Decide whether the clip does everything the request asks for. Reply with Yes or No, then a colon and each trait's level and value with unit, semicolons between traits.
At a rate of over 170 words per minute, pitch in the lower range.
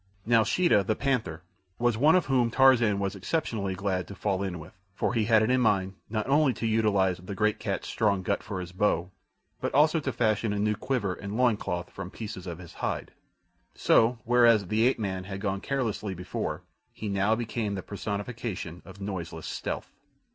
Yes: average, 190 wpm; low, 105 Hz